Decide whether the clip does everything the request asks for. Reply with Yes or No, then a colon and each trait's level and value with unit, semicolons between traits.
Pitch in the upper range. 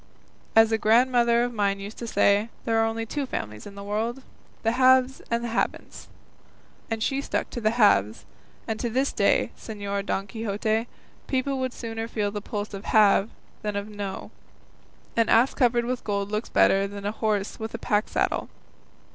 Yes: high, 220 Hz